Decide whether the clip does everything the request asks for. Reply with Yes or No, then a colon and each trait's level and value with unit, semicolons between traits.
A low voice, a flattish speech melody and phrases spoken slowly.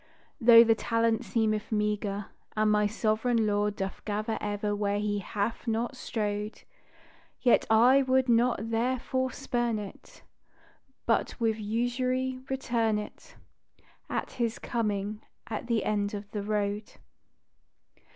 No: high, 220 Hz; narrow, 2.3 semitones; slow, 125 wpm